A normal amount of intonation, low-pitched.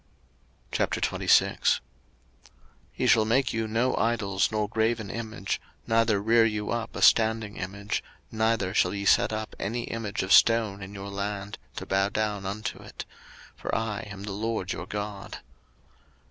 No: narrow, 2.1 semitones; low, 110 Hz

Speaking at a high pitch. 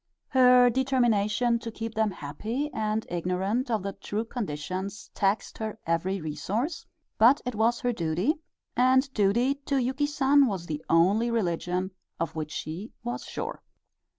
Yes: high, 220 Hz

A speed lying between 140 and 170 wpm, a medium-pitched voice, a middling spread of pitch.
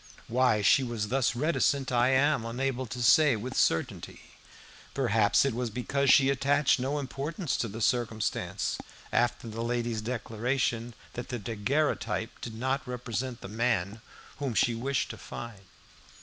No: average, 150 wpm; low, 120 Hz; average, 3.0 semitones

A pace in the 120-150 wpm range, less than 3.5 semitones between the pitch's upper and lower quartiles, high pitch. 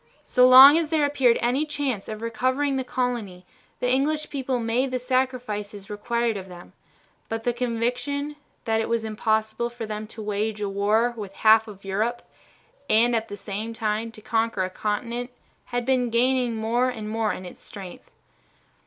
No: average, 170 wpm; average, 2.8 semitones; high, 230 Hz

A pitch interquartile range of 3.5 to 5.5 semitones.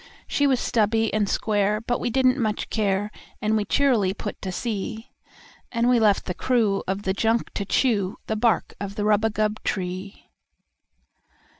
No: narrow, 2.5 semitones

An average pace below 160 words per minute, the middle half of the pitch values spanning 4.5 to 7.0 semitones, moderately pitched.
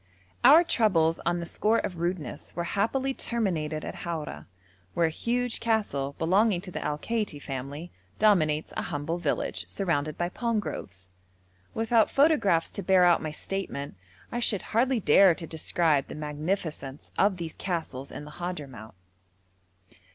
Yes: average, 150 wpm; wide, 5.6 semitones; medium, 175 Hz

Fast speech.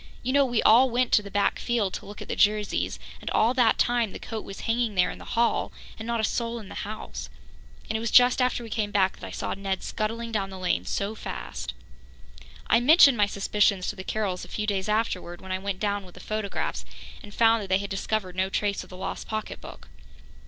Yes: fast, 235 wpm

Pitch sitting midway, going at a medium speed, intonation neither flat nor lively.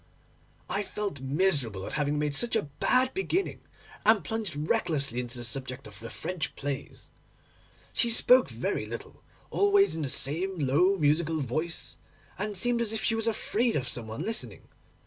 No: medium, 165 Hz; average, 165 wpm; wide, 8.0 semitones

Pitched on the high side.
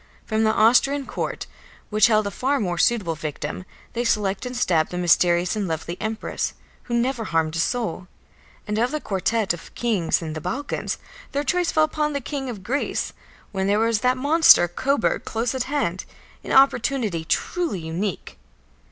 Yes: high, 220 Hz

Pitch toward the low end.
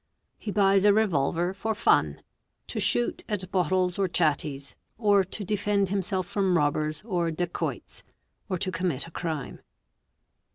No: medium, 185 Hz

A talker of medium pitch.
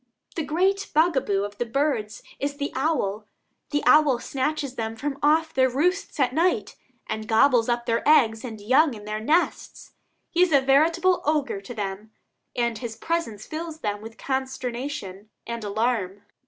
No: very high, 260 Hz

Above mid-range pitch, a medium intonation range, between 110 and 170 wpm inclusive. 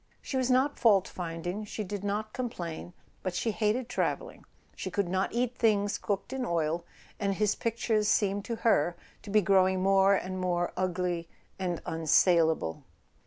Yes: high, 195 Hz; average, 3.4 semitones; average, 165 wpm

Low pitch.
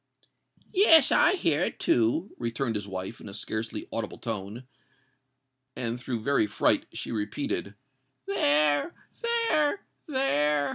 Yes: low, 130 Hz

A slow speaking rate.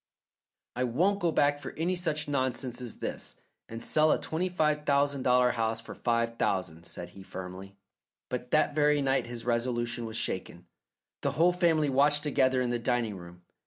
No: average, 180 wpm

